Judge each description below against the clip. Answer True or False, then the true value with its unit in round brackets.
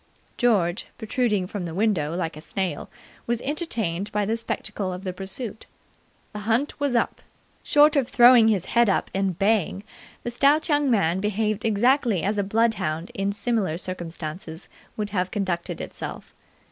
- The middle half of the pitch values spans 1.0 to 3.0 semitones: False (4.2 semitones)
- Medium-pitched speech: False (205 Hz)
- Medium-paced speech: True (160 wpm)